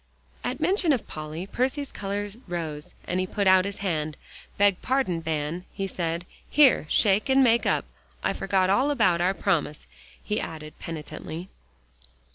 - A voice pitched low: No, medium, 185 Hz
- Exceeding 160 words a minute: No, average, 155 wpm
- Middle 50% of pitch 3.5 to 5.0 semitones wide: Yes, average, 4.4 semitones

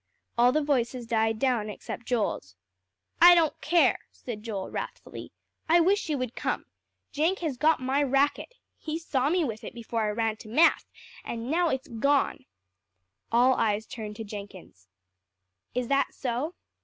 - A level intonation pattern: No, average, 5.2 semitones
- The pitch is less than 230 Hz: No, very high, 250 Hz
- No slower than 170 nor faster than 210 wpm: No, average, 160 wpm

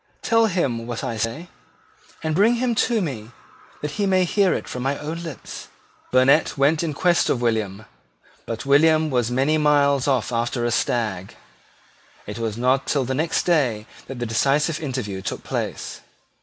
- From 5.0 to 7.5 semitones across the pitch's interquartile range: Yes, average, 5.3 semitones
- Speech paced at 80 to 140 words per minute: No, average, 170 wpm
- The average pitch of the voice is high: No, low, 135 Hz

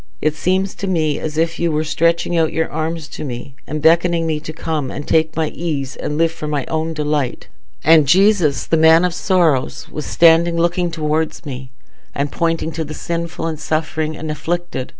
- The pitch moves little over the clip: Yes, narrow, 1.7 semitones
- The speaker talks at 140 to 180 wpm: No, average, 195 wpm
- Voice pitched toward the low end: No, medium, 160 Hz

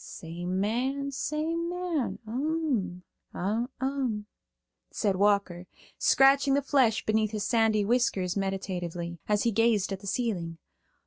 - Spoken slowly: Yes, slow, 115 wpm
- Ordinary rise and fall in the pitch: No, wide, 5.9 semitones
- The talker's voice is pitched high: Yes, high, 220 Hz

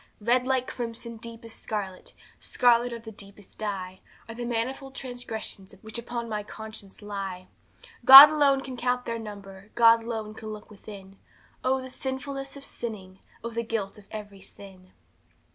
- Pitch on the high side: Yes, high, 225 Hz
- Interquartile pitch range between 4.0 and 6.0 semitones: No, average, 3.3 semitones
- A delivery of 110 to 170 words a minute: Yes, average, 160 wpm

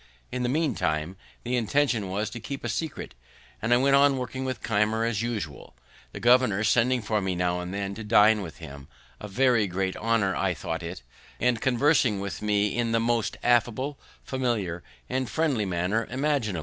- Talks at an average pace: Yes, average, 190 wpm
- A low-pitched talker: Yes, low, 115 Hz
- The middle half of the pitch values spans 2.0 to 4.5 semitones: Yes, average, 4.1 semitones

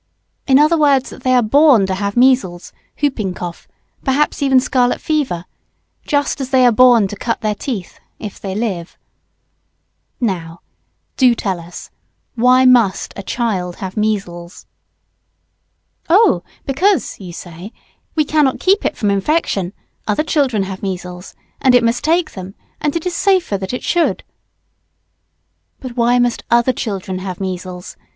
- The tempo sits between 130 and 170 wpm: Yes, average, 150 wpm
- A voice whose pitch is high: Yes, high, 235 Hz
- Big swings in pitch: Yes, wide, 6.0 semitones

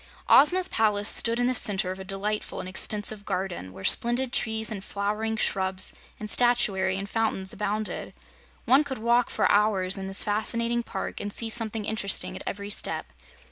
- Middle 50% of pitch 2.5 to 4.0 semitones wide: Yes, average, 3.1 semitones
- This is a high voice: Yes, high, 210 Hz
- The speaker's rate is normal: Yes, average, 175 wpm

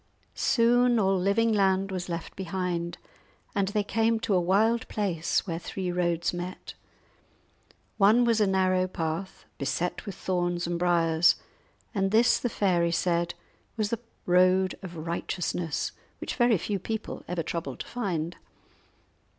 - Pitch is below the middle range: No, medium, 185 Hz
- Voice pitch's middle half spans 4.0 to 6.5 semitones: No, average, 3.2 semitones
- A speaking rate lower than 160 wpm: Yes, average, 140 wpm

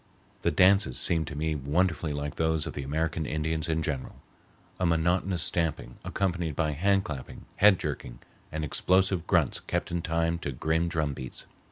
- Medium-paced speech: Yes, average, 170 wpm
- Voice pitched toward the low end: Yes, very low, 80 Hz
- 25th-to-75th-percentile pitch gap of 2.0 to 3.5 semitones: Yes, narrow, 2.6 semitones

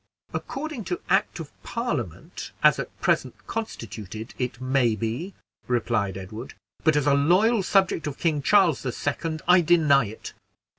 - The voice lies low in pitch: No, medium, 145 Hz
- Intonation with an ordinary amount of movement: No, wide, 7.3 semitones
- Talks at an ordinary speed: Yes, average, 150 wpm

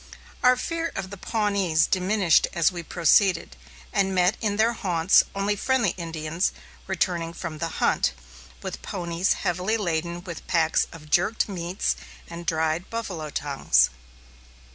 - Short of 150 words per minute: Yes, average, 140 wpm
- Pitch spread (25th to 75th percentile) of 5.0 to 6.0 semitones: No, average, 3.3 semitones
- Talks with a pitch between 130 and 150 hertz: No, medium, 180 Hz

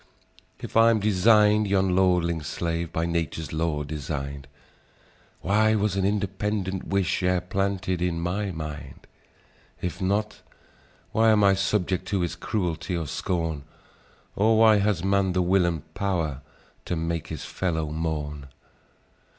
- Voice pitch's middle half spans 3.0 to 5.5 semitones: Yes, average, 3.4 semitones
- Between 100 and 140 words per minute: Yes, slow, 135 wpm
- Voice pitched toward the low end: Yes, very low, 90 Hz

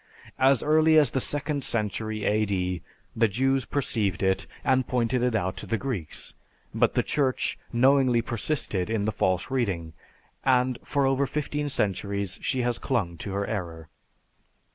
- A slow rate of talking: No, average, 155 wpm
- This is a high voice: No, low, 115 Hz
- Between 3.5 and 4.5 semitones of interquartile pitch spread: No, average, 5.1 semitones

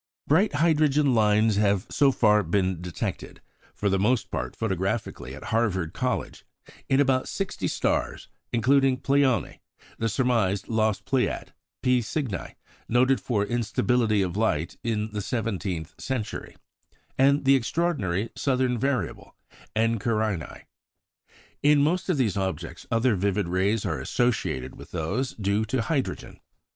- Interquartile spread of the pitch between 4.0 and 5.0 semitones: Yes, average, 4.7 semitones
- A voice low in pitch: Yes, low, 115 Hz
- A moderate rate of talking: No, slow, 130 wpm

